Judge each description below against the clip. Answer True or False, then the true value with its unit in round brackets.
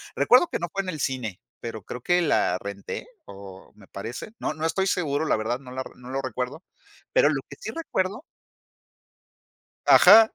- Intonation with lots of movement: True (8.2 semitones)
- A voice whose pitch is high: False (135 Hz)